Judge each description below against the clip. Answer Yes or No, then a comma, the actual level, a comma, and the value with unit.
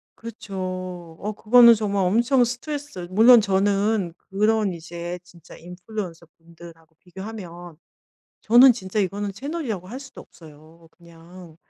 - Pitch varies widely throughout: No, average, 4.4 semitones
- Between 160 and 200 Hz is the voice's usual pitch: Yes, high, 190 Hz